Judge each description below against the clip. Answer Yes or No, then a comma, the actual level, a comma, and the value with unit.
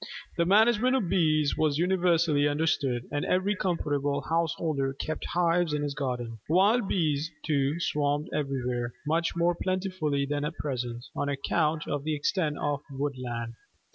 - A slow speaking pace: No, average, 145 wpm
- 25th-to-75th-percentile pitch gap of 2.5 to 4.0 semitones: Yes, average, 3.4 semitones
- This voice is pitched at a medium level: Yes, medium, 150 Hz